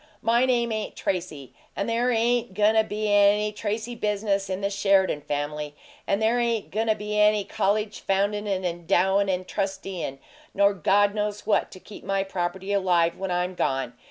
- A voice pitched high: Yes, high, 200 Hz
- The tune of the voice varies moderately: No, narrow, 2.3 semitones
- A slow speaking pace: No, average, 180 wpm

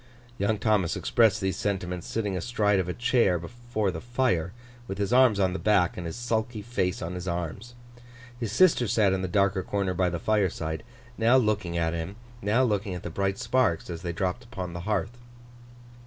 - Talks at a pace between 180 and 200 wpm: Yes, average, 195 wpm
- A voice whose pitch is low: Yes, low, 100 Hz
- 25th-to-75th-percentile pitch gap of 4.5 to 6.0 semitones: No, average, 3.9 semitones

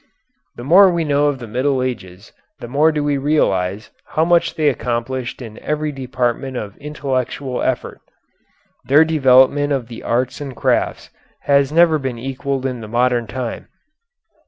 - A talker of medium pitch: No, low, 130 Hz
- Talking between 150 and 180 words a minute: Yes, average, 155 wpm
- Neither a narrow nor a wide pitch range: Yes, average, 3.3 semitones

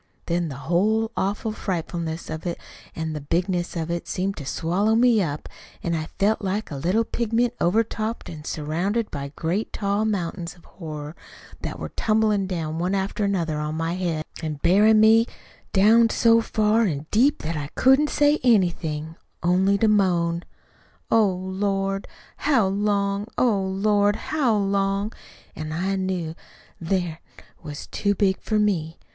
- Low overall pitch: No, high, 190 Hz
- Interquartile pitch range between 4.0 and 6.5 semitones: Yes, average, 4.3 semitones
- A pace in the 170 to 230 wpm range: No, average, 160 wpm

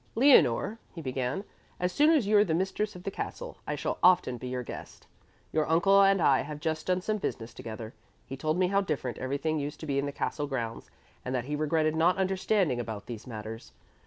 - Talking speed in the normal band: No, fast, 220 wpm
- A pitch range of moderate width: No, wide, 6.8 semitones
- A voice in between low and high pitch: Yes, medium, 155 Hz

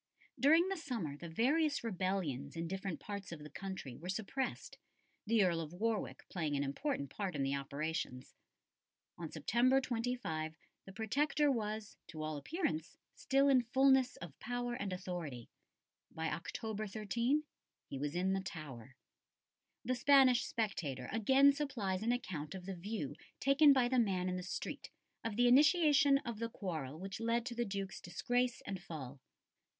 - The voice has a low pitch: No, high, 200 Hz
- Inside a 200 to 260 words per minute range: No, average, 160 wpm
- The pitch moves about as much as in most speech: No, wide, 7.3 semitones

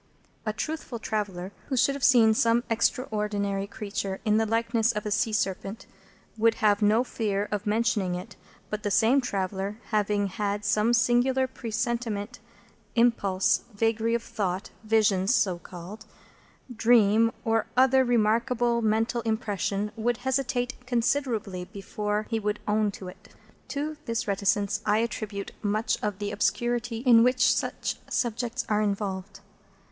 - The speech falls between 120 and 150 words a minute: Yes, average, 140 wpm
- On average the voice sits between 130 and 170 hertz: No, high, 220 Hz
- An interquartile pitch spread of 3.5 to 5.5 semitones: No, narrow, 2.5 semitones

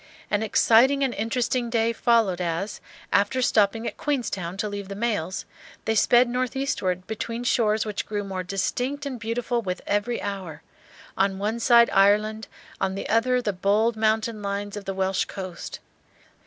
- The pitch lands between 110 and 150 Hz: No, high, 215 Hz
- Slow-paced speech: No, average, 160 wpm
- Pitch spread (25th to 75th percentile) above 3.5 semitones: No, average, 3.1 semitones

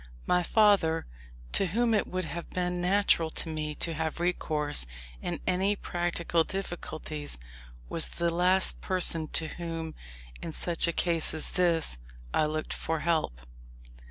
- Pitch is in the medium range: Yes, medium, 170 Hz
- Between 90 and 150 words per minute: Yes, average, 145 wpm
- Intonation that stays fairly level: Yes, narrow, 2.1 semitones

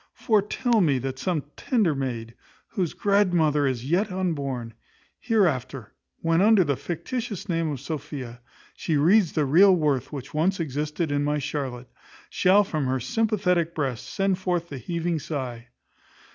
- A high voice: No, medium, 155 Hz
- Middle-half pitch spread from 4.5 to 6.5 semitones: Yes, wide, 5.5 semitones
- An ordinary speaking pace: Yes, average, 145 wpm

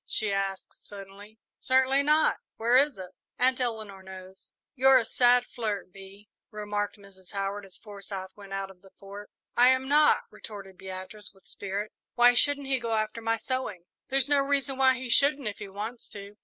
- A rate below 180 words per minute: No, average, 185 wpm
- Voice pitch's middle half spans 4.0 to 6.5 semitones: Yes, average, 4.8 semitones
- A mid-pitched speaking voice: No, high, 215 Hz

